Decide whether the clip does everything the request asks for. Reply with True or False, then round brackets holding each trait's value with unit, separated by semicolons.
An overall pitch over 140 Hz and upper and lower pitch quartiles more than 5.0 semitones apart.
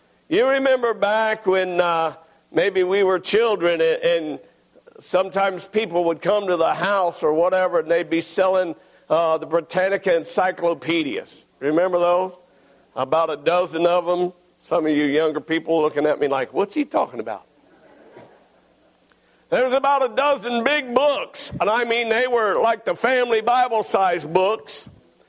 True (185 Hz; 5.5 semitones)